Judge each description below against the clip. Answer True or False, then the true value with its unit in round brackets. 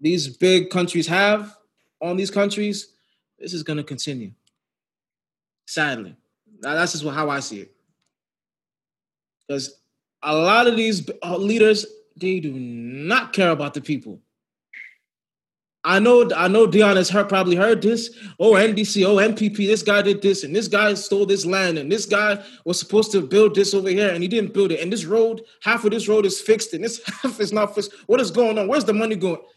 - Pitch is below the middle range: False (200 Hz)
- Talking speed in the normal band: True (190 wpm)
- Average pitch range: True (3.4 semitones)